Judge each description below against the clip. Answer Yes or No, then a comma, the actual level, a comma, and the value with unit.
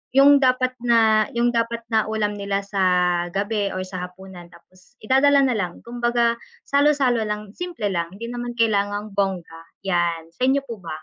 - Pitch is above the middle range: Yes, high, 215 Hz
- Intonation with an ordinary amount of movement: Yes, average, 3.8 semitones